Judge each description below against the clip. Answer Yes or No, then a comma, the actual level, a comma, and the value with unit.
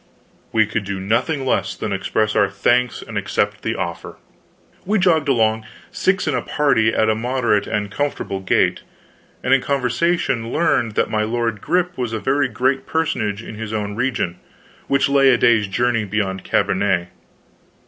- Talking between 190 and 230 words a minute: No, average, 170 wpm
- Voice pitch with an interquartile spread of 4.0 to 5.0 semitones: Yes, average, 4.4 semitones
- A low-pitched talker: Yes, low, 115 Hz